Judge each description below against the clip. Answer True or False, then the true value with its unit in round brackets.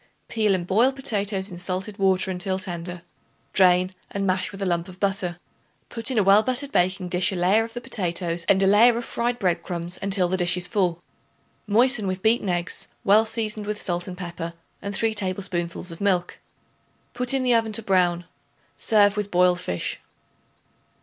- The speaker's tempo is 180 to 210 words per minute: True (185 wpm)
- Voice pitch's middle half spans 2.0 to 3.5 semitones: True (3.1 semitones)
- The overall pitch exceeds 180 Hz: True (190 Hz)